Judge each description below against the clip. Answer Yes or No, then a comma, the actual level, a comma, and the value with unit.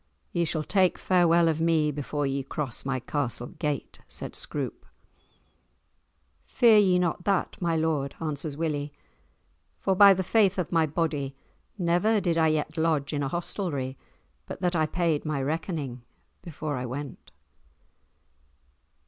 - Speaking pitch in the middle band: Yes, medium, 160 Hz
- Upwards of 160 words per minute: No, average, 145 wpm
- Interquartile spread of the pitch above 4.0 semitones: No, average, 3.4 semitones